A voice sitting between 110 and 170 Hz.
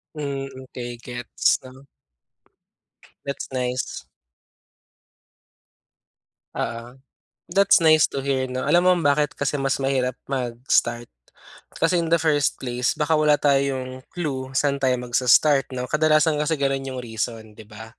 Yes: low, 135 Hz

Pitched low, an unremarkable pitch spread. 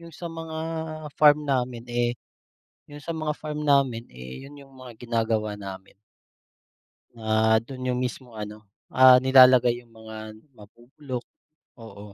Yes: low, 125 Hz; average, 3.9 semitones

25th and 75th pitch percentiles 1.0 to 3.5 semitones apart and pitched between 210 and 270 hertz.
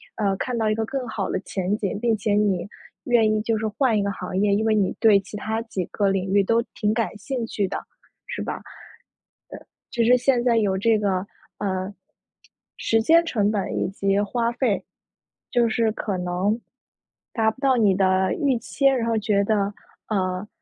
Yes: average, 2.8 semitones; high, 215 Hz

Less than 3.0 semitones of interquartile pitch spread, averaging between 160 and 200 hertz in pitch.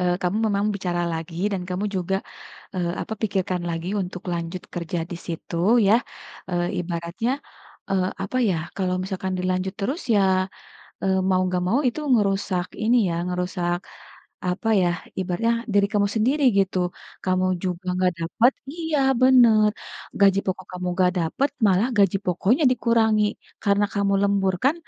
Yes: narrow, 2.6 semitones; high, 190 Hz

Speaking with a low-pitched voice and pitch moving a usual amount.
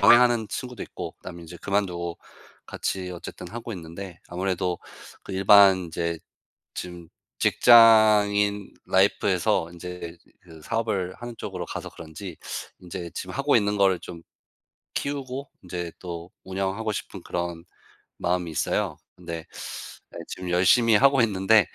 Yes: very low, 95 Hz; average, 3.6 semitones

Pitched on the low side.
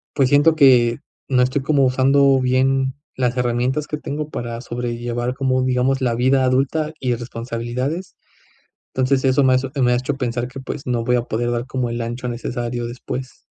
Yes: low, 130 Hz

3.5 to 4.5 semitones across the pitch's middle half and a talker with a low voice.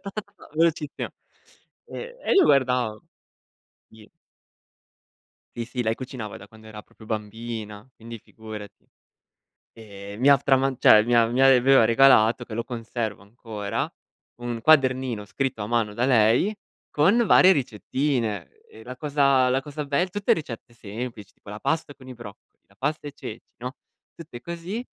Yes: average, 4.1 semitones; low, 120 Hz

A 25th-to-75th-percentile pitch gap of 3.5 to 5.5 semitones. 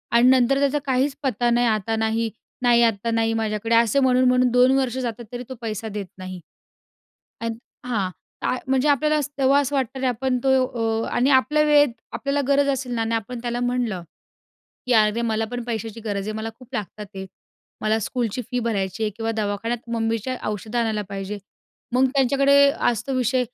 No: average, 2.8 semitones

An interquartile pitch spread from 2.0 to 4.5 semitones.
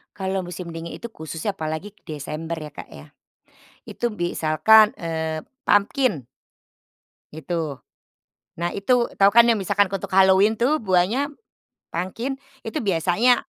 No: average, 5.1 semitones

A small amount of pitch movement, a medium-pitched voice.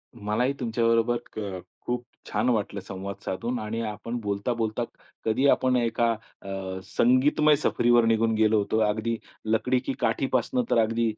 No: narrow, 2.2 semitones; low, 115 Hz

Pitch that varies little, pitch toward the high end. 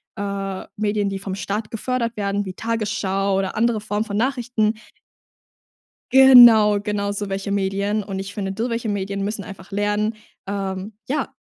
Yes: narrow, 2.0 semitones; high, 205 Hz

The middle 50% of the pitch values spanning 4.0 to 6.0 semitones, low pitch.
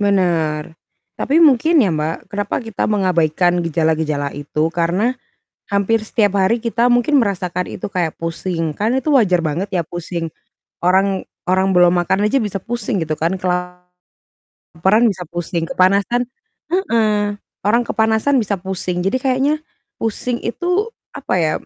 No: average, 4.7 semitones; high, 190 Hz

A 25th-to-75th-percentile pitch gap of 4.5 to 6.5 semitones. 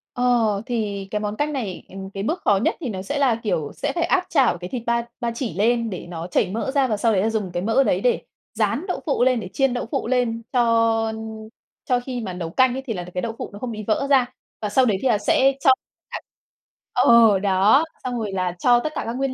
No: average, 4.1 semitones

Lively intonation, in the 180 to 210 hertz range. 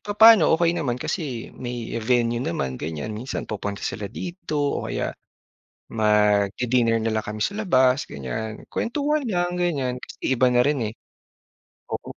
No: wide, 7.5 semitones; low, 125 Hz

